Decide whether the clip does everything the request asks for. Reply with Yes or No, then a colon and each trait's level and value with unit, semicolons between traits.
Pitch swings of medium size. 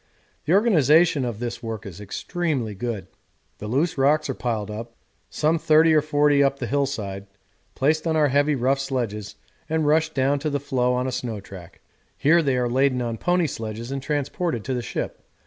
Yes: average, 4.6 semitones